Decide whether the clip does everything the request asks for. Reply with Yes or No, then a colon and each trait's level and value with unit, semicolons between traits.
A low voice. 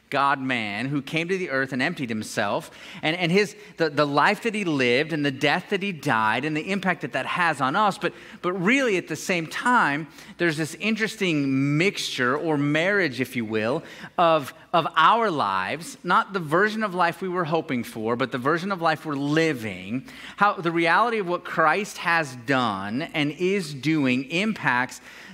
No: medium, 160 Hz